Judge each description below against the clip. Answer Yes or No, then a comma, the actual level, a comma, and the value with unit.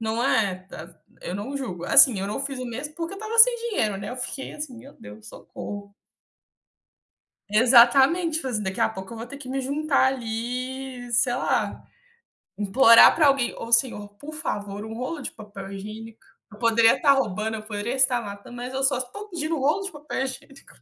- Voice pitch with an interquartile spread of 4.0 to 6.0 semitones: Yes, average, 4.4 semitones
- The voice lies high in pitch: Yes, high, 245 Hz